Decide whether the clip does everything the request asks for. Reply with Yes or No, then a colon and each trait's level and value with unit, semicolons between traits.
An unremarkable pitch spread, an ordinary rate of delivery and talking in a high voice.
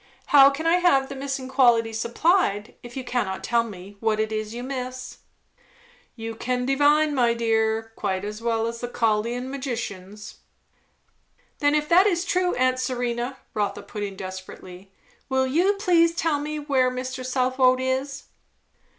Yes: average, 3.7 semitones; average, 160 wpm; very high, 255 Hz